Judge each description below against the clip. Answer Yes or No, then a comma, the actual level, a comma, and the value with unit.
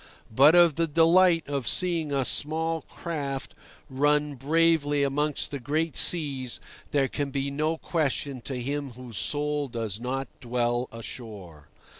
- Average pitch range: Yes, average, 3.4 semitones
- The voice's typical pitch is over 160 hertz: No, medium, 145 Hz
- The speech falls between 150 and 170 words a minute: No, average, 140 wpm